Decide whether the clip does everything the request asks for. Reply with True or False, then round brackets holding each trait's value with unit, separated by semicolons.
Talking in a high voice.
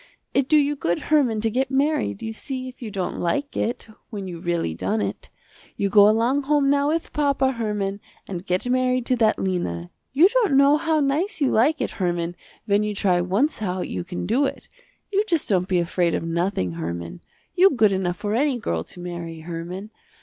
True (210 Hz)